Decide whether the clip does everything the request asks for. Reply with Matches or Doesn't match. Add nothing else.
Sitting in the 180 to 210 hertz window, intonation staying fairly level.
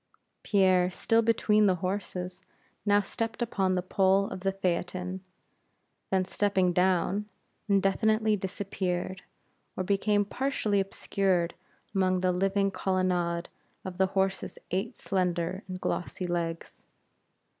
Matches